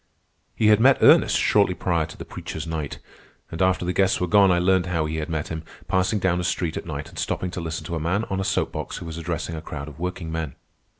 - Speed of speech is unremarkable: No, fast, 255 wpm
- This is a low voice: Yes, very low, 85 Hz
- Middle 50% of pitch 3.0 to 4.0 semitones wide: No, narrow, 2.6 semitones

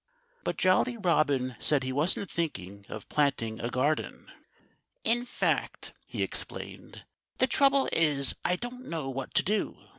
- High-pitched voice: No, medium, 150 Hz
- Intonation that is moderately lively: No, wide, 7.5 semitones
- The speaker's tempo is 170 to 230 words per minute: No, average, 145 wpm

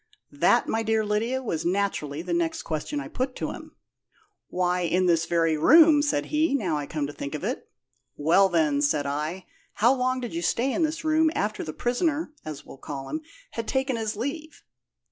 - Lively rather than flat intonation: Yes, wide, 8.8 semitones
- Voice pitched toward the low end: No, high, 205 Hz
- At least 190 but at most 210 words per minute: Yes, average, 200 wpm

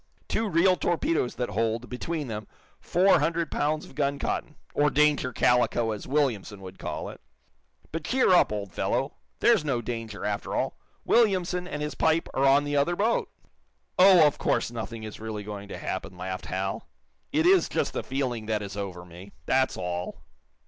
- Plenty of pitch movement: Yes, wide, 7.4 semitones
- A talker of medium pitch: No, low, 130 Hz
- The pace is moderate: Yes, average, 180 wpm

